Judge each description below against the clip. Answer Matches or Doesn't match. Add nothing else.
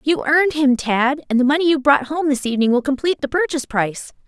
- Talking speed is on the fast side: Matches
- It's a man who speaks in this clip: Doesn't match